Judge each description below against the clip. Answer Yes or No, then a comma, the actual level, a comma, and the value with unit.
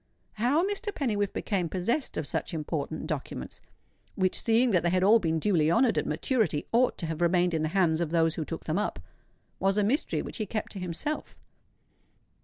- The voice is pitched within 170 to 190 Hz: Yes, medium, 185 Hz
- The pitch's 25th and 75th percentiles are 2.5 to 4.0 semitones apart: No, wide, 5.6 semitones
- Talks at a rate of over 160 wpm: Yes, average, 190 wpm